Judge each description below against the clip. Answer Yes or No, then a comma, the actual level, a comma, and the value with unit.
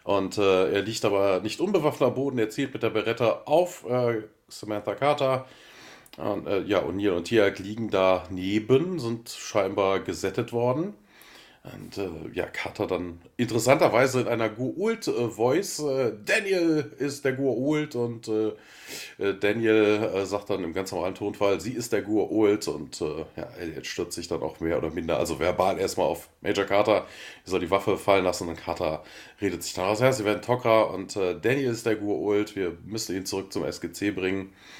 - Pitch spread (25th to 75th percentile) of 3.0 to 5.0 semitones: Yes, average, 4.1 semitones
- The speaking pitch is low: Yes, low, 110 Hz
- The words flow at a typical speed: Yes, average, 180 wpm